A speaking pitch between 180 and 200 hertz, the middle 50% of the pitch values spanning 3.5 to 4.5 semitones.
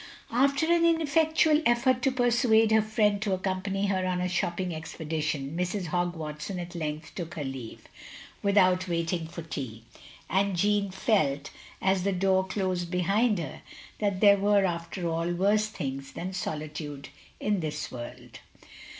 Yes: medium, 185 Hz; average, 4.2 semitones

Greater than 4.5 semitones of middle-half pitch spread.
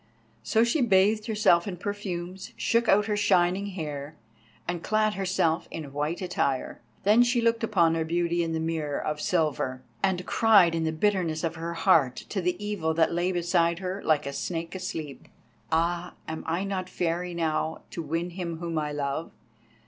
No: average, 3.3 semitones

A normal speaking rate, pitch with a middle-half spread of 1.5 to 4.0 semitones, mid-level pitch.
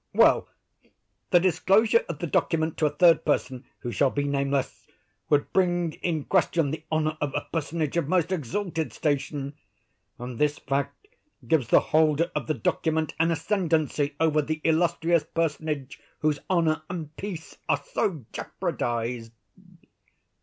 Yes: average, 145 wpm; average, 2.9 semitones; medium, 155 Hz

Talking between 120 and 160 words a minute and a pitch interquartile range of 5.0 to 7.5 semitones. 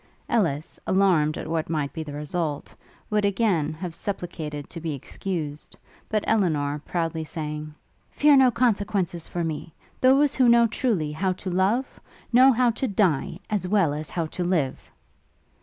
Yes: average, 155 wpm; wide, 5.5 semitones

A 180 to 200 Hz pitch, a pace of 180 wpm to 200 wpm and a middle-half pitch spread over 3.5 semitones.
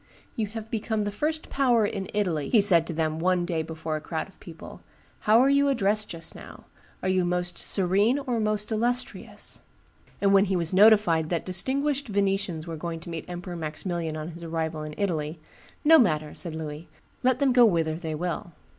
Yes: medium, 185 Hz; average, 195 wpm; average, 4.9 semitones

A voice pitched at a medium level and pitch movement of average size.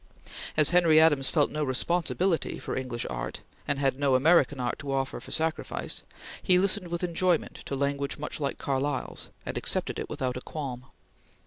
Yes: medium, 145 Hz; average, 3.9 semitones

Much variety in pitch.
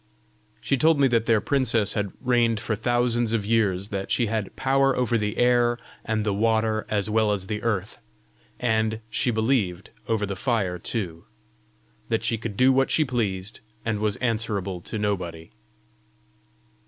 No: average, 2.8 semitones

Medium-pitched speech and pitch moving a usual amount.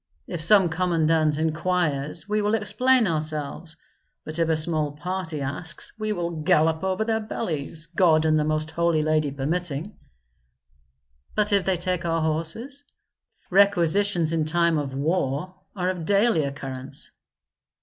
Yes: medium, 165 Hz; average, 3.2 semitones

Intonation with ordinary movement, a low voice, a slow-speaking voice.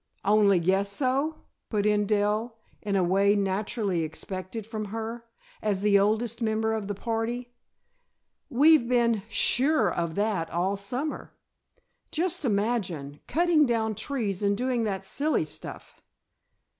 No: average, 3.3 semitones; high, 215 Hz; slow, 130 wpm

